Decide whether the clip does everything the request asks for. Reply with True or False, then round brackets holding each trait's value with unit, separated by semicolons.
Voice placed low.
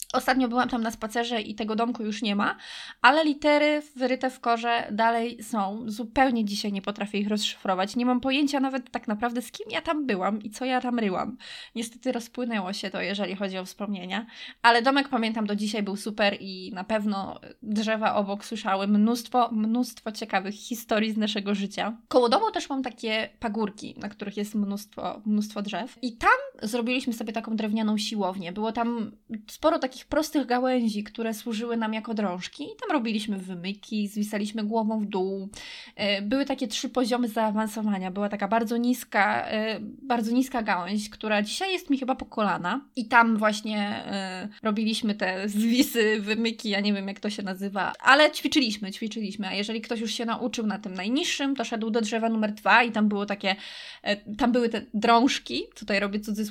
False (225 Hz)